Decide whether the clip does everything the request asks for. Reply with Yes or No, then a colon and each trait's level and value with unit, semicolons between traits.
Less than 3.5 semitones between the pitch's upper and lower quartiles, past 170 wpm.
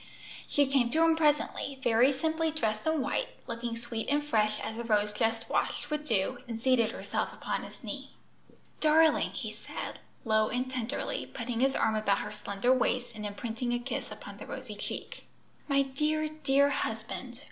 No: average, 4.3 semitones; average, 180 wpm